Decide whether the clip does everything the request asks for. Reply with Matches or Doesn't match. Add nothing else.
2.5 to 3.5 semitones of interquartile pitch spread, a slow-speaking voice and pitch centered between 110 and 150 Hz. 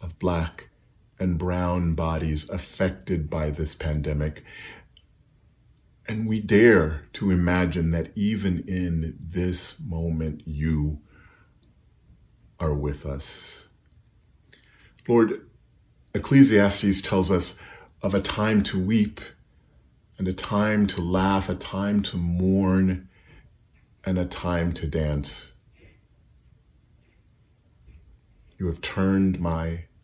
Doesn't match